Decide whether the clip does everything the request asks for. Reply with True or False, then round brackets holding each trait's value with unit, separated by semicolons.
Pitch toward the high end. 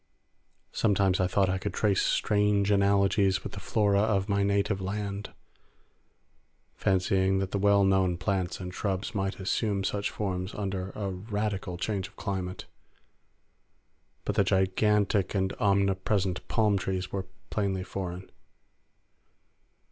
False (100 Hz)